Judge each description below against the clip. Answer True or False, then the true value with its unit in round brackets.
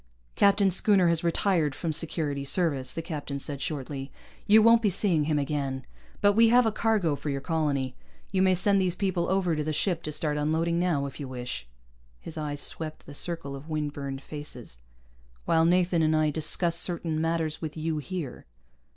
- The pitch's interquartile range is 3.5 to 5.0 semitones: True (3.8 semitones)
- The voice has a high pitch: False (160 Hz)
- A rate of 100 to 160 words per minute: False (190 wpm)